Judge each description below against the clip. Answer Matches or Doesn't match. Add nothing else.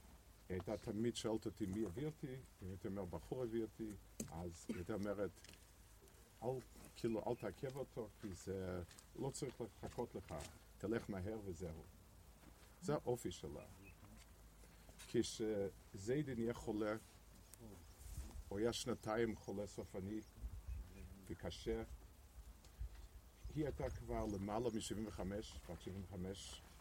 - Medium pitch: Doesn't match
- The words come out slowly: Matches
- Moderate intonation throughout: Matches